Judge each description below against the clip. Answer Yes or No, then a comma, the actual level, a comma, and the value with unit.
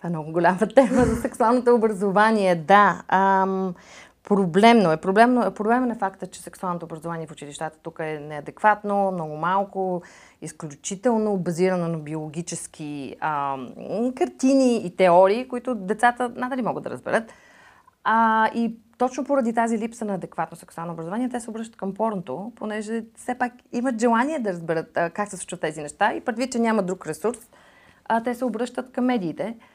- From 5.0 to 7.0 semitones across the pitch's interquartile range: Yes, wide, 5.4 semitones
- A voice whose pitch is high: Yes, high, 205 Hz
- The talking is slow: No, average, 160 wpm